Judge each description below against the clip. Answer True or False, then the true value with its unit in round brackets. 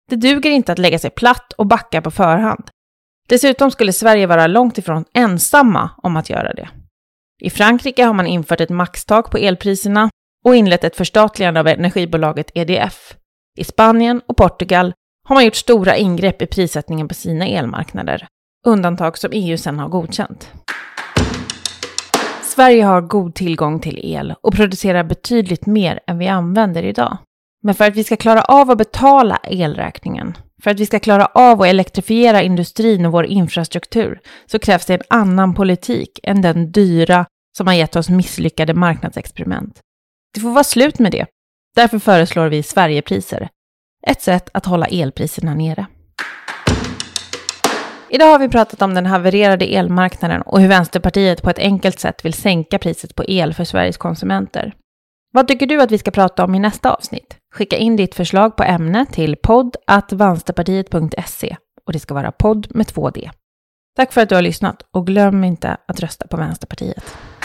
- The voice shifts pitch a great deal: False (4.3 semitones)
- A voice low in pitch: False (190 Hz)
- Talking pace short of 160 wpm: False (165 wpm)